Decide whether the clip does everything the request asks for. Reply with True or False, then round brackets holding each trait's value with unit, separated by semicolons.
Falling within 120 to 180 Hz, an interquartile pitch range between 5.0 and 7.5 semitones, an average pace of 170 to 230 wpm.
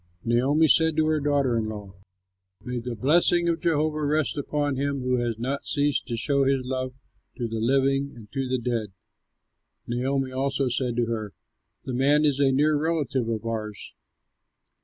False (135 Hz; 3.3 semitones; 175 wpm)